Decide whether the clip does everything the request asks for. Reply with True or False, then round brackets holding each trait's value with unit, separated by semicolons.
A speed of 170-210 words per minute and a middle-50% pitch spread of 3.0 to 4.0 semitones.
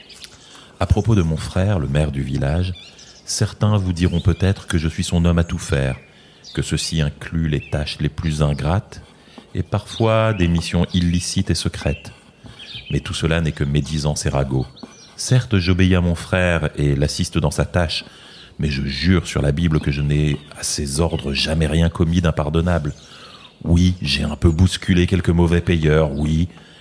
True (175 wpm; 3.7 semitones)